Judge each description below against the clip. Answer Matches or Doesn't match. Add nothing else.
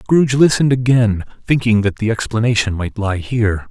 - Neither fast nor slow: Matches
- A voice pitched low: Matches